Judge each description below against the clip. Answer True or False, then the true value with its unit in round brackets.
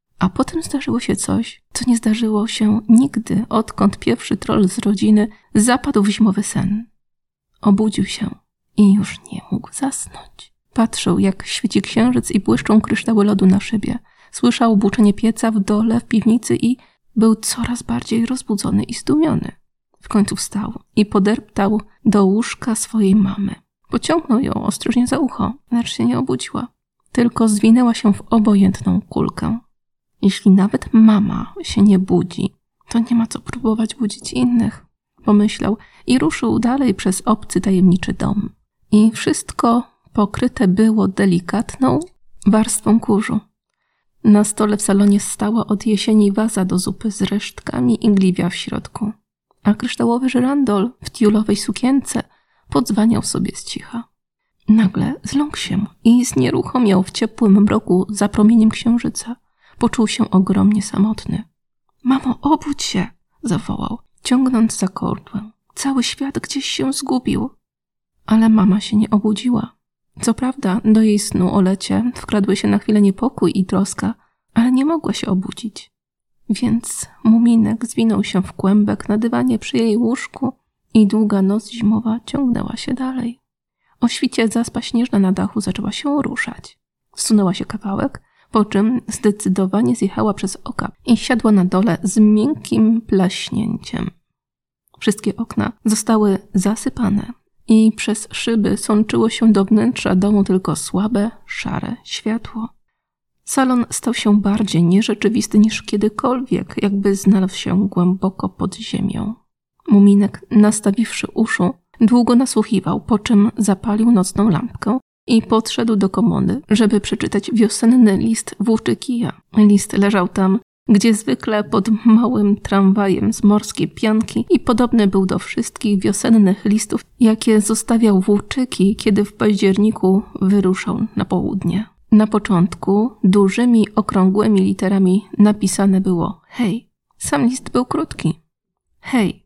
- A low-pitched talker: False (215 Hz)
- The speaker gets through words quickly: False (135 wpm)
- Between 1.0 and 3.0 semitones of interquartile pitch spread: True (2.6 semitones)